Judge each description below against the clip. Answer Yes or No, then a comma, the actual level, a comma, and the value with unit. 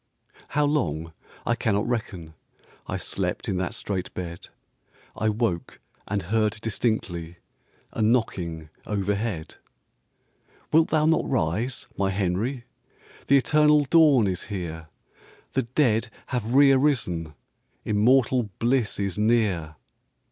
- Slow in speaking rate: Yes, slow, 115 wpm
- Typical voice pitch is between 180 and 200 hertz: No, low, 110 Hz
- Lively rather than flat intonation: Yes, wide, 5.7 semitones